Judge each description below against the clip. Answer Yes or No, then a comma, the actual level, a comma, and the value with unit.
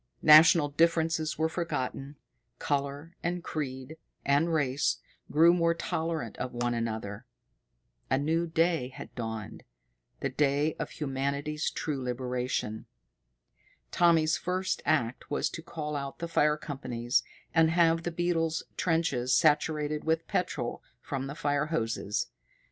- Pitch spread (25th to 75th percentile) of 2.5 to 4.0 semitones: Yes, average, 3.7 semitones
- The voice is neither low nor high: Yes, medium, 150 Hz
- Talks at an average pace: No, slow, 125 wpm